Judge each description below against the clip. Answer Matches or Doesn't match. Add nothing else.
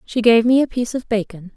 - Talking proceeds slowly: Doesn't match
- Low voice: Doesn't match